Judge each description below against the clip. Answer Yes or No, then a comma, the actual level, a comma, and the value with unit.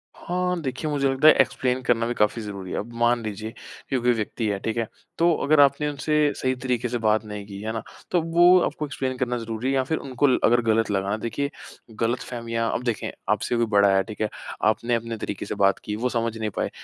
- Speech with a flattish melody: No, average, 3.4 semitones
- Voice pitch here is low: Yes, low, 120 Hz